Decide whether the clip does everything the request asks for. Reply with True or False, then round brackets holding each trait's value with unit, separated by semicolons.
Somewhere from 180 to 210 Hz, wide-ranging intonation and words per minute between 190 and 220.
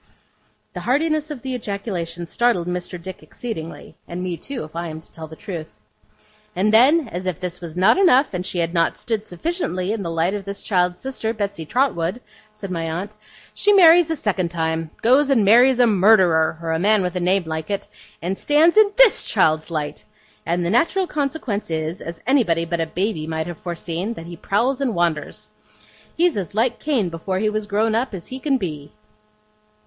True (190 Hz; 6.4 semitones; 200 wpm)